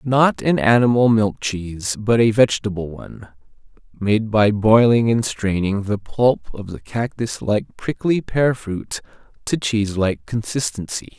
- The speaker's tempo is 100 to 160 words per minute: Yes, slow, 135 wpm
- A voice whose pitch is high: No, low, 110 Hz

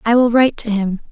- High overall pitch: Yes, high, 225 Hz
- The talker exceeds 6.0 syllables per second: Yes, 6.5 syllables/s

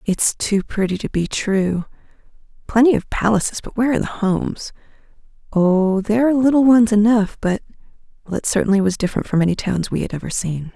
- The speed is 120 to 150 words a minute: No, average, 175 wpm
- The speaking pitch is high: Yes, high, 205 Hz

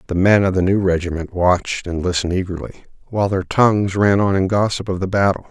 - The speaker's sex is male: Yes, male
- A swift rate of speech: Yes, fast, 220 wpm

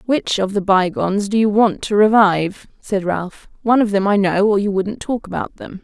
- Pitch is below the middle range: No, high, 200 Hz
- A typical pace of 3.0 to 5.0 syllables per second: No, 5.2 syllables/s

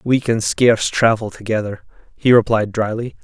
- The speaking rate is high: No, average, 150 wpm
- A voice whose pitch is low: Yes, low, 110 Hz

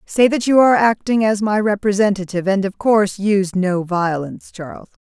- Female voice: Yes, female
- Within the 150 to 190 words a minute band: Yes, average, 180 wpm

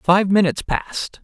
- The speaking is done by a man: Yes, male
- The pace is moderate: Yes, average, 145 wpm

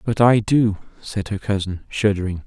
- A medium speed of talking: Yes, average, 170 wpm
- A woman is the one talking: No, male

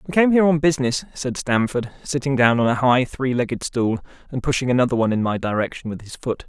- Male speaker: Yes, male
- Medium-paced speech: No, fast, 230 wpm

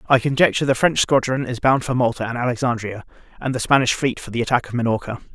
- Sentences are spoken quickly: Yes, fast, 225 wpm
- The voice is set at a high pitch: No, low, 125 Hz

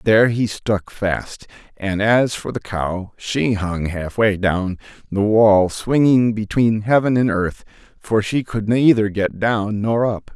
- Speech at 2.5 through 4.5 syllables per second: Yes, 3.7 syllables/s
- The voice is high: No, low, 105 Hz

